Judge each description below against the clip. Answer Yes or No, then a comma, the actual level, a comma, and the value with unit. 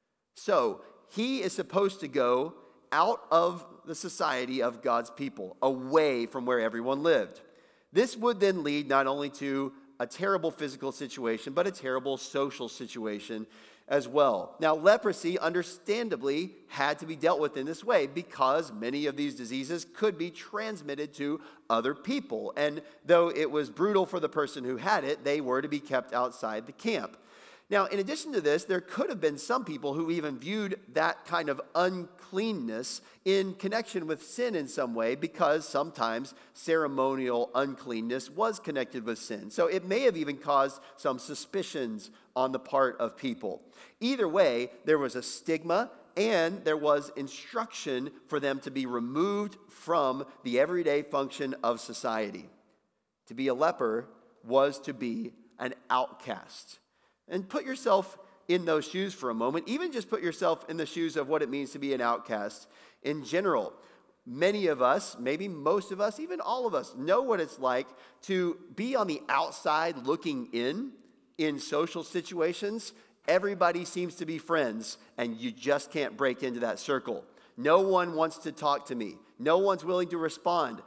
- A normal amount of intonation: No, wide, 5.9 semitones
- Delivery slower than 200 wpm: Yes, average, 170 wpm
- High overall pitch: No, medium, 155 Hz